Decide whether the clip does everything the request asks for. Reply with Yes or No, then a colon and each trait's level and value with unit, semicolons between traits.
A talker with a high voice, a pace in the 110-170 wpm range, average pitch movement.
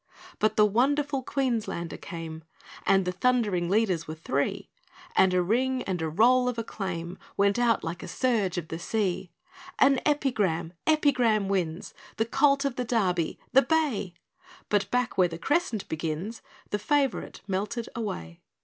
No: high, 210 Hz; average, 155 wpm; wide, 6.0 semitones